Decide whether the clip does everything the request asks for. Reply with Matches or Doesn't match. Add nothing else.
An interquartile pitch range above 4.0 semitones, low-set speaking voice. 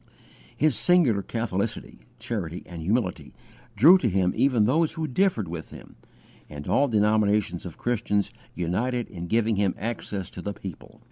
Matches